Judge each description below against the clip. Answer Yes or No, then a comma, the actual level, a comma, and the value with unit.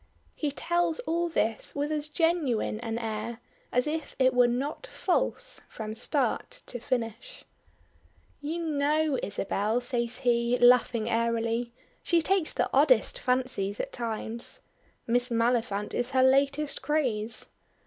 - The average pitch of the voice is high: Yes, very high, 250 Hz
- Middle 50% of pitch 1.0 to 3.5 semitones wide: No, average, 4.7 semitones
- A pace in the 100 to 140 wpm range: Yes, slow, 135 wpm